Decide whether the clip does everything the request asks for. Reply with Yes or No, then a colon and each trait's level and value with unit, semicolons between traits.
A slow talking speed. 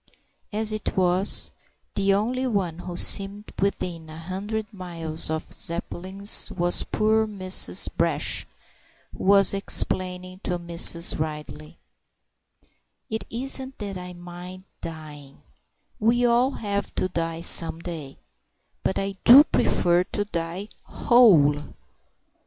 Yes: slow, 120 wpm